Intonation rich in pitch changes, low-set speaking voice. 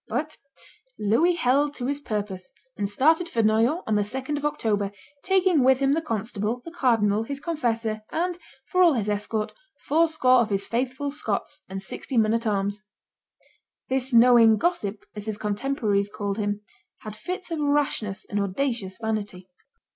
No: wide, 5.7 semitones; high, 230 Hz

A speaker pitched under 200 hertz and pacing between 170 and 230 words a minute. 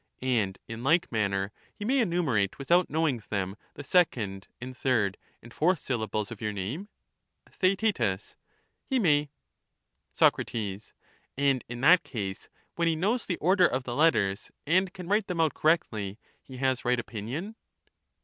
No: low, 135 Hz; average, 155 wpm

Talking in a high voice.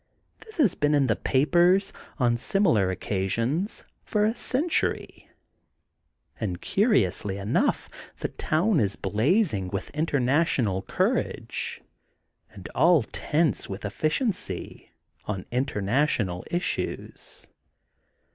No: low, 135 Hz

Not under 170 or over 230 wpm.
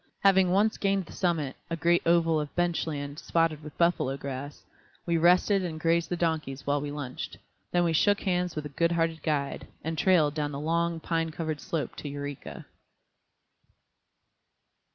Yes: average, 175 wpm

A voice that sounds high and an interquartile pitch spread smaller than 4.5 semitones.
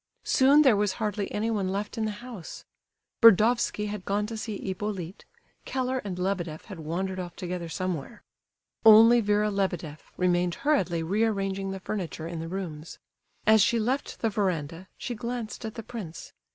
Yes: high, 200 Hz; average, 3.6 semitones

